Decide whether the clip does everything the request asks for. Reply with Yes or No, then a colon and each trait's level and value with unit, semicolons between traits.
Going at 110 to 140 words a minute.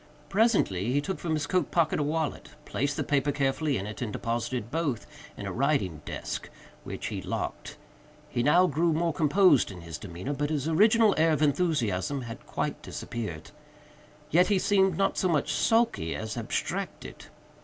No: average, 175 wpm